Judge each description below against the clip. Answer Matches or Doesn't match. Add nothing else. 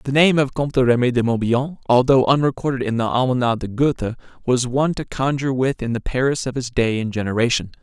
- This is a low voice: Matches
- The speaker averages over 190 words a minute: Matches